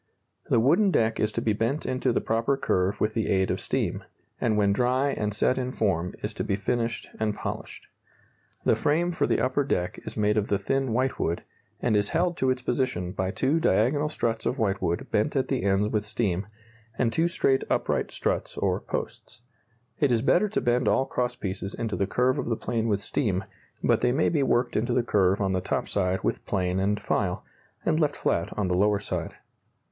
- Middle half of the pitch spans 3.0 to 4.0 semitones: No, average, 4.5 semitones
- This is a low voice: Yes, low, 115 Hz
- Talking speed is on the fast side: Yes, fast, 210 wpm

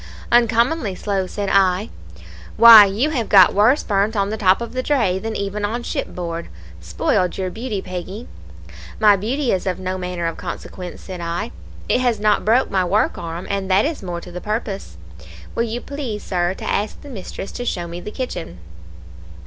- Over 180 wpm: Yes, average, 190 wpm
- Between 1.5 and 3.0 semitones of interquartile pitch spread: No, average, 4.0 semitones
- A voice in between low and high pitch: No, high, 200 Hz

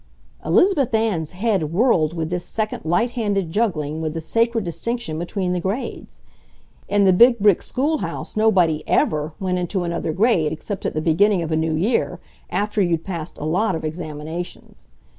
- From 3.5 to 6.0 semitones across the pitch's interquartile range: Yes, average, 5.2 semitones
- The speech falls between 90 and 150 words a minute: No, average, 170 wpm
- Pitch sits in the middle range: Yes, medium, 180 Hz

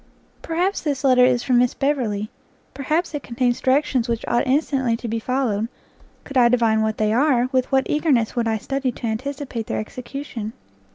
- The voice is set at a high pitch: Yes, very high, 250 Hz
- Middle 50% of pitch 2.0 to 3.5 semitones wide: Yes, average, 3.2 semitones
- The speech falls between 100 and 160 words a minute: No, average, 180 wpm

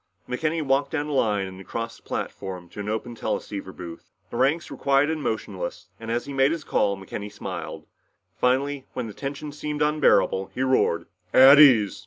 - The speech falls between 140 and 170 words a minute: No, average, 190 wpm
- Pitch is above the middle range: No, low, 125 Hz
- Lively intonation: Yes, wide, 5.8 semitones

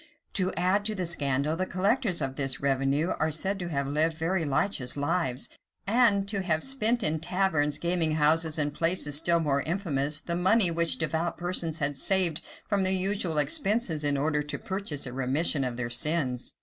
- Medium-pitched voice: Yes, medium, 160 Hz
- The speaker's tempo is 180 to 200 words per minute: Yes, average, 190 wpm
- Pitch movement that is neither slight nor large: Yes, average, 4.3 semitones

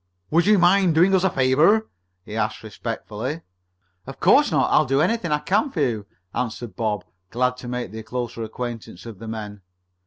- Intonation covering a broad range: Yes, wide, 7.0 semitones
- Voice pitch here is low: Yes, low, 125 Hz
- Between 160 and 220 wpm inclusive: Yes, average, 185 wpm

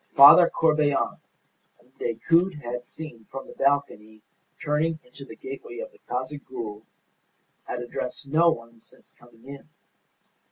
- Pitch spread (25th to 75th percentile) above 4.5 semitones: Yes, average, 5.1 semitones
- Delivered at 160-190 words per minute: No, slow, 135 wpm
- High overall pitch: No, medium, 140 Hz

